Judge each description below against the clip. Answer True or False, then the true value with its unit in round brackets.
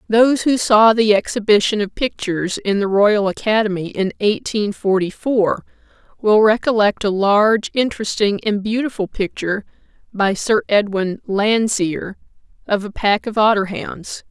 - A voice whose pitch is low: False (210 Hz)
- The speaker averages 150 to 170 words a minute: False (140 wpm)